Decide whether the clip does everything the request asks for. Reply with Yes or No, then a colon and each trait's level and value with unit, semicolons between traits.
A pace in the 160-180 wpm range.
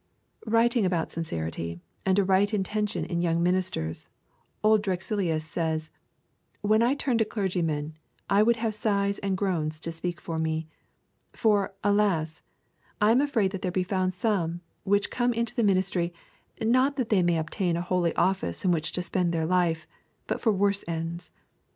Yes: average, 170 wpm